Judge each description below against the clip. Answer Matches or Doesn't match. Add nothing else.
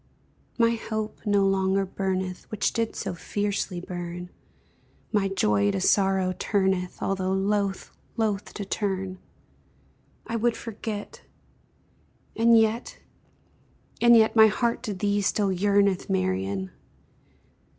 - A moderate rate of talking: Doesn't match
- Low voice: Doesn't match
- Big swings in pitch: Doesn't match